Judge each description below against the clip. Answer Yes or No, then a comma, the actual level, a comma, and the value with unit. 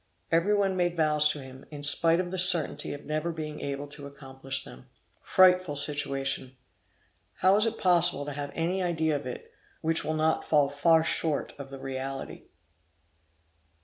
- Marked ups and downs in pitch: No, average, 3.4 semitones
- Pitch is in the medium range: Yes, medium, 150 Hz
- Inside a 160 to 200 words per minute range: Yes, average, 170 wpm